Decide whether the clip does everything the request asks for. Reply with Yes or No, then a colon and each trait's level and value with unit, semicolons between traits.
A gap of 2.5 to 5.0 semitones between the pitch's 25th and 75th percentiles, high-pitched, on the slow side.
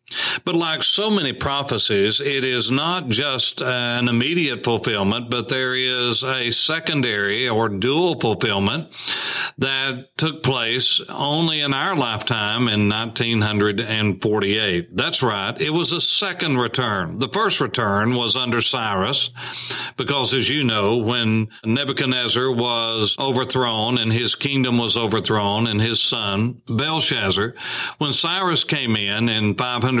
No: average, 3.4 semitones; low, 125 Hz; slow, 130 wpm